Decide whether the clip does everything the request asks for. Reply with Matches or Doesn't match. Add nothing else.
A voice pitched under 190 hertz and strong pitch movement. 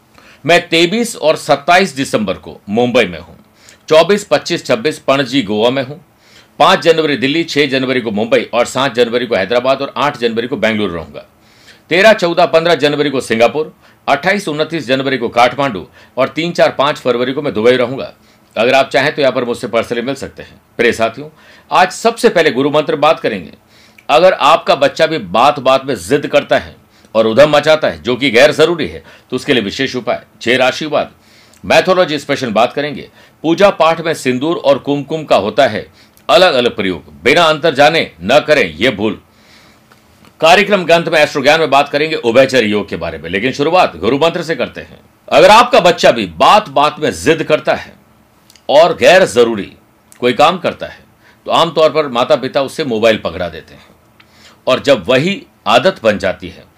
Doesn't match